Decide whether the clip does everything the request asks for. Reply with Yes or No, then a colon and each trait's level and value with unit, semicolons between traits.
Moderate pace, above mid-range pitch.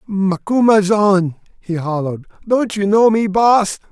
No: slow, 125 wpm; high, 200 Hz